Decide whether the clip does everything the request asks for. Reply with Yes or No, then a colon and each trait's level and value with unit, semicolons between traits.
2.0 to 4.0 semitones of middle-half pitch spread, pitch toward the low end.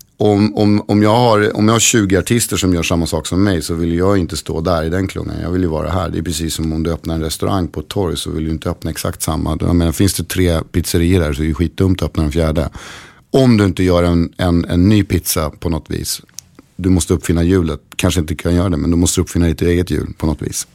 Yes: average, 2.8 semitones; very low, 90 Hz